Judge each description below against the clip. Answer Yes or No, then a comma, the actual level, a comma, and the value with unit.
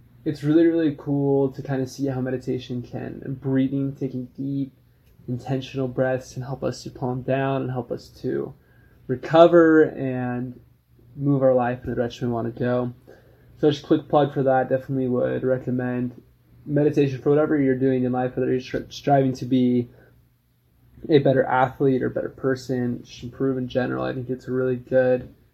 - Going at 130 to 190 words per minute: Yes, average, 180 wpm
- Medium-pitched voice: No, low, 130 Hz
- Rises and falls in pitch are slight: Yes, narrow, 1.6 semitones